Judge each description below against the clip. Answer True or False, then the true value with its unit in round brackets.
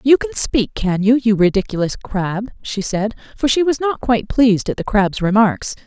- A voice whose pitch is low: False (220 Hz)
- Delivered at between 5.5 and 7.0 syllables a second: False (5.0 syllables/s)